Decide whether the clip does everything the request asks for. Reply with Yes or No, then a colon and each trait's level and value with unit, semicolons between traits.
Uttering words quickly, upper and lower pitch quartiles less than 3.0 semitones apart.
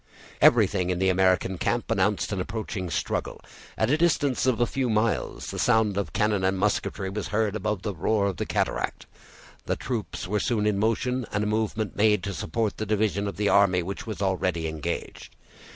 No: average, 195 wpm; narrow, 2.6 semitones